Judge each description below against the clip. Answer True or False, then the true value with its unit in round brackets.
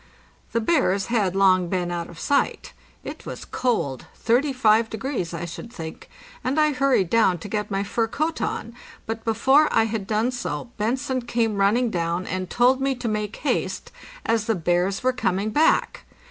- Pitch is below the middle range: False (220 Hz)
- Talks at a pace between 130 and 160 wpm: False (175 wpm)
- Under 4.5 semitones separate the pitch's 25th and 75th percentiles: False (5.1 semitones)